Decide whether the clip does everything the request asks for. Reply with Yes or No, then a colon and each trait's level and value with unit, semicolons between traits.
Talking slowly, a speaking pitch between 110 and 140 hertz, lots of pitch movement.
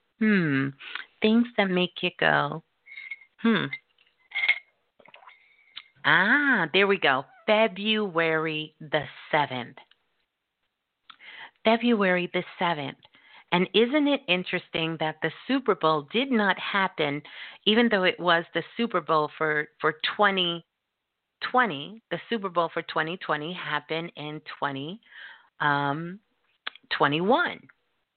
No: slow, 110 wpm; medium, 180 Hz; wide, 5.8 semitones